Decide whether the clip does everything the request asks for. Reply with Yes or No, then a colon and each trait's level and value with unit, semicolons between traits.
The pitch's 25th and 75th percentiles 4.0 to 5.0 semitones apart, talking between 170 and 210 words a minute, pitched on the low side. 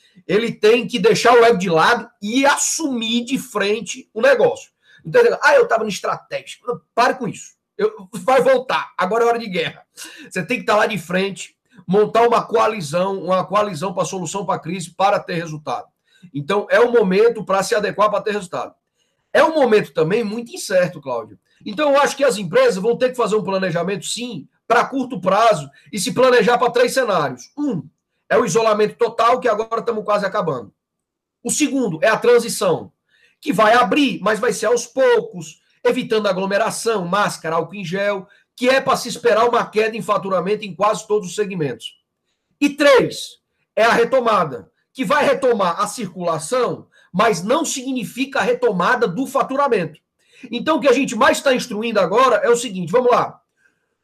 No: average, 4.3 semitones; fast, 185 wpm; high, 225 Hz